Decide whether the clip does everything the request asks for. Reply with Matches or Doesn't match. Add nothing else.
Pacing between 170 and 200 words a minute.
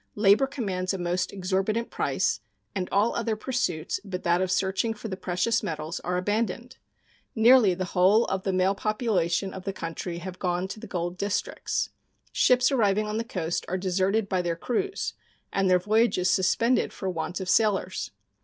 Matches